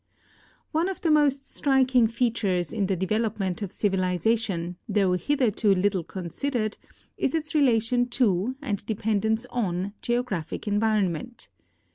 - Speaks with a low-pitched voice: No, high, 220 Hz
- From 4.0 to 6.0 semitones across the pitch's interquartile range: Yes, average, 4.5 semitones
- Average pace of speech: No, slow, 125 wpm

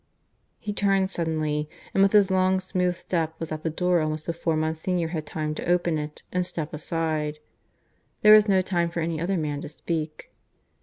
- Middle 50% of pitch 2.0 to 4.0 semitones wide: Yes, average, 2.9 semitones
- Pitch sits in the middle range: Yes, medium, 165 Hz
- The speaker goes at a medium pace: Yes, average, 190 wpm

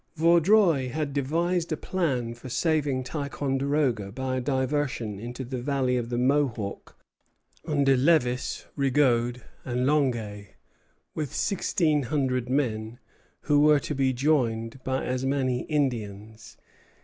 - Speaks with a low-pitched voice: Yes, low, 130 Hz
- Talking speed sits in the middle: No, slow, 125 wpm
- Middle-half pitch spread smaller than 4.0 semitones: Yes, average, 3.2 semitones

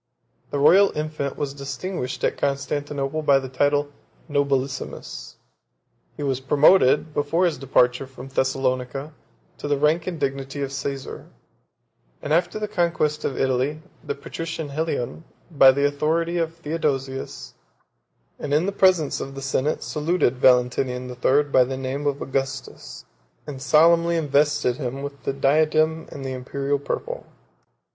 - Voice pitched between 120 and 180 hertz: Yes, medium, 140 Hz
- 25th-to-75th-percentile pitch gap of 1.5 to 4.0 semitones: Yes, narrow, 2.6 semitones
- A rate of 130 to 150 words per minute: Yes, average, 145 wpm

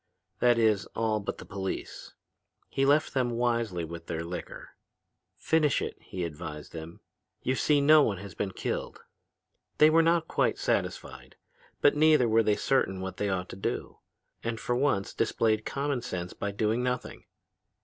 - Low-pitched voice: Yes, low, 115 Hz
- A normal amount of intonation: No, wide, 6.1 semitones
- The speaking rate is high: No, average, 165 wpm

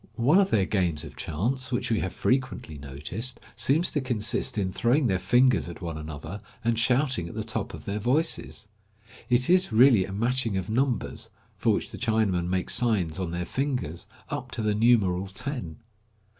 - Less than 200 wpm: Yes, average, 185 wpm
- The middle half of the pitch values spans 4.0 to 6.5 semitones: Yes, wide, 5.5 semitones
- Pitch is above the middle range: No, low, 110 Hz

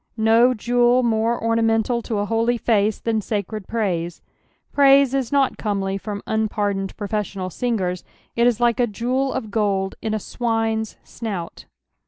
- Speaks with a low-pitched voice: No, high, 220 Hz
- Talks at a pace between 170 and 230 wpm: No, average, 155 wpm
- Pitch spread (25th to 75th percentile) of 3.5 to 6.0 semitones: No, average, 2.7 semitones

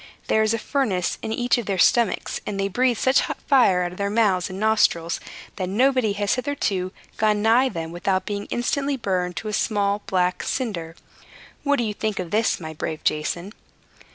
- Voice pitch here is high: Yes, high, 205 Hz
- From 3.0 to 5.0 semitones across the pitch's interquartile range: Yes, average, 4.3 semitones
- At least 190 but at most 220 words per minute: Yes, average, 195 wpm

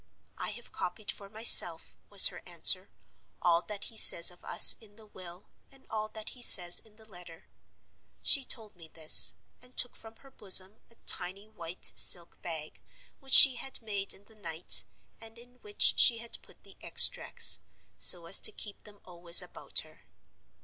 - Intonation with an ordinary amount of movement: Yes, average, 4.3 semitones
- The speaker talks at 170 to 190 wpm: Yes, average, 180 wpm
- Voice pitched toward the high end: Yes, high, 205 Hz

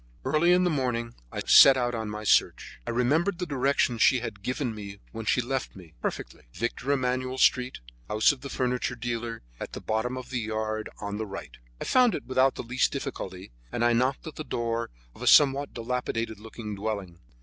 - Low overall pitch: Yes, low, 120 Hz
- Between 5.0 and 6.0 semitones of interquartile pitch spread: No, average, 3.1 semitones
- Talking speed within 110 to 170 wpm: No, average, 200 wpm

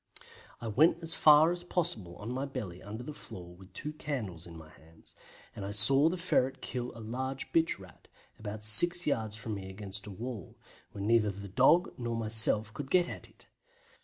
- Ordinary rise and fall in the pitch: No, wide, 6.1 semitones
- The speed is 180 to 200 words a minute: Yes, average, 195 wpm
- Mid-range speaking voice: No, low, 115 Hz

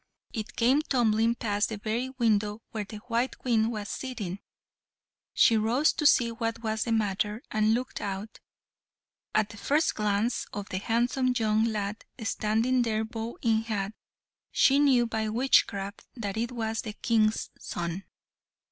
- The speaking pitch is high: Yes, high, 220 Hz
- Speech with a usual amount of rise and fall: No, narrow, 2.1 semitones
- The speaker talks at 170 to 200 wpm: No, average, 155 wpm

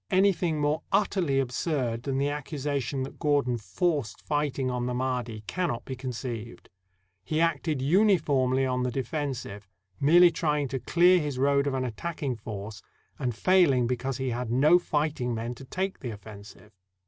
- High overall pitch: No, low, 135 Hz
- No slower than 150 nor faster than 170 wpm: Yes, average, 165 wpm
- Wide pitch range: No, average, 3.8 semitones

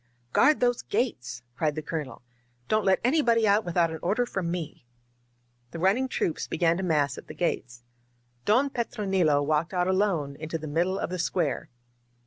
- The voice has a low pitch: No, medium, 175 Hz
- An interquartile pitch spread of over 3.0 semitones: Yes, average, 5.2 semitones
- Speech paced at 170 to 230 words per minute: Yes, average, 180 wpm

